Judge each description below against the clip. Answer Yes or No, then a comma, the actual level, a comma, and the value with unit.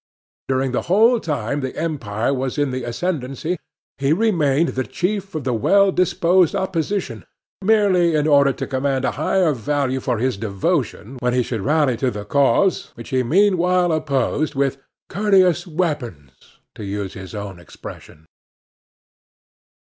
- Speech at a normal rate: Yes, average, 150 wpm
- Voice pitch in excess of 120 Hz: Yes, medium, 140 Hz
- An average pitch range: No, wide, 6.1 semitones